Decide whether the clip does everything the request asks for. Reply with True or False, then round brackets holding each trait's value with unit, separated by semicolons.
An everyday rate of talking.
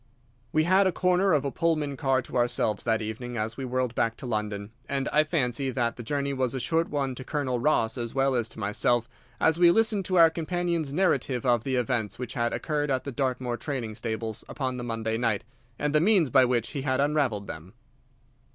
False (215 wpm)